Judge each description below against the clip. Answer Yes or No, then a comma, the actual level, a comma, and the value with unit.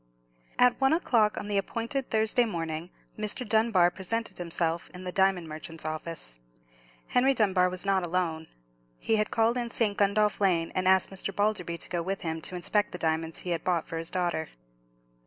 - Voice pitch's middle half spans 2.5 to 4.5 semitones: Yes, average, 4.2 semitones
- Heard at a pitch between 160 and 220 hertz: Yes, medium, 185 Hz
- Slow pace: No, average, 185 wpm